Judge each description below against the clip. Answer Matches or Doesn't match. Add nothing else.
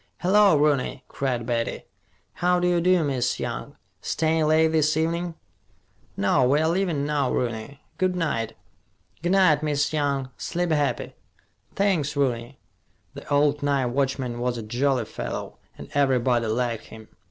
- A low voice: Doesn't match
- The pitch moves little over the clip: Doesn't match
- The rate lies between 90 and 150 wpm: Matches